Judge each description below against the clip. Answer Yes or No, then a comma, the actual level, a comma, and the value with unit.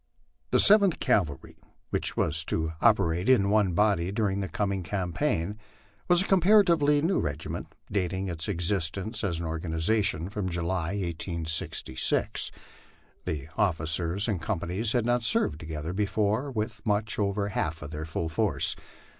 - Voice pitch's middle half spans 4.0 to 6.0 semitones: Yes, average, 4.6 semitones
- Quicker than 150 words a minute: No, average, 140 wpm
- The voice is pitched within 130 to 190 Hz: No, very low, 95 Hz